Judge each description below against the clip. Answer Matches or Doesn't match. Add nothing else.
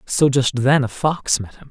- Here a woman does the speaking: Doesn't match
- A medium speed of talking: Doesn't match